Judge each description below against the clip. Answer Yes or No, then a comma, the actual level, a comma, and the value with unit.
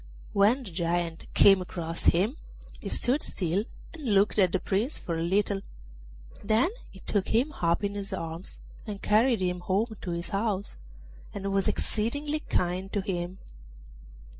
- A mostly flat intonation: No, average, 3.5 semitones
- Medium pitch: No, high, 195 Hz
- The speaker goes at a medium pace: Yes, average, 160 wpm